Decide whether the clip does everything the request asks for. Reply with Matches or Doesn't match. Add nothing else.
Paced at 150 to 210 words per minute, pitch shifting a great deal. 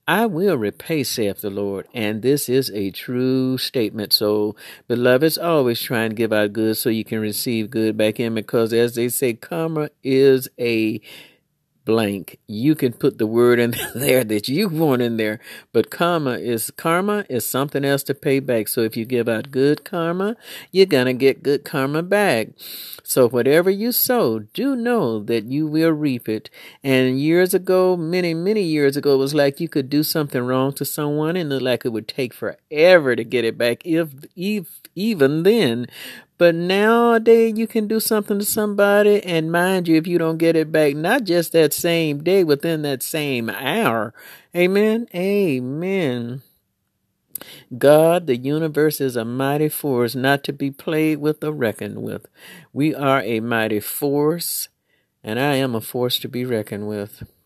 Matches